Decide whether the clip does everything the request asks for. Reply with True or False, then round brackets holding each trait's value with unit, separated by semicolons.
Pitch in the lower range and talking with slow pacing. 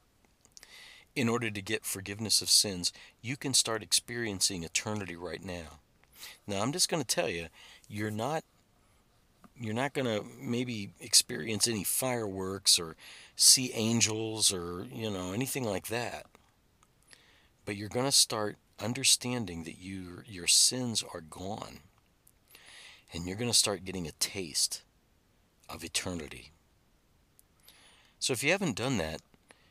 True (105 Hz; 130 wpm)